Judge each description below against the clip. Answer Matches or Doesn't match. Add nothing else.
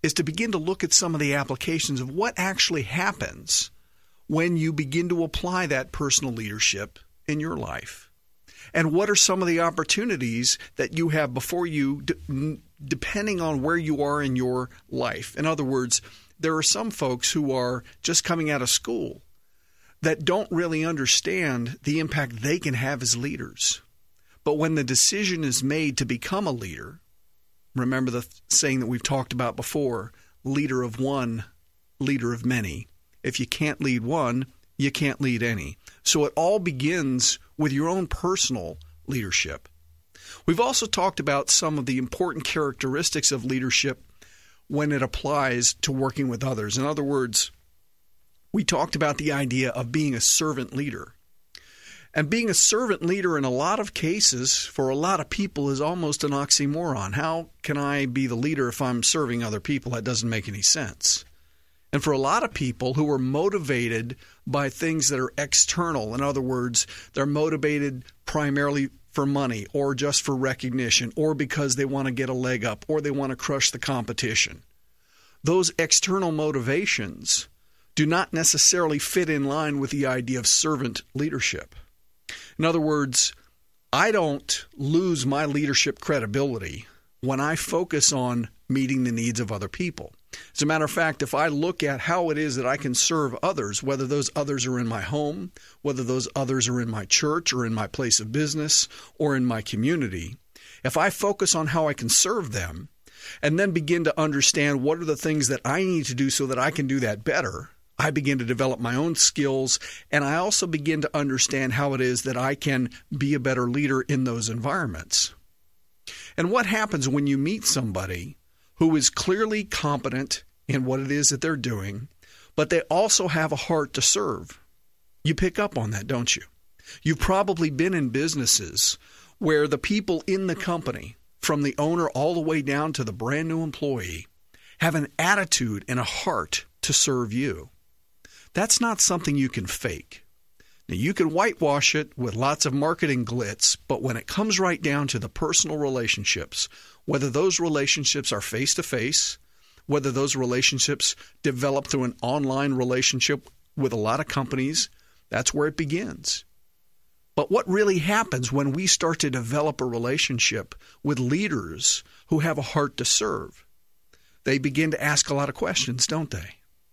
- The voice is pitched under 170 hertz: Matches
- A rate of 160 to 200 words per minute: Matches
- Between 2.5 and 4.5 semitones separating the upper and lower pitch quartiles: Matches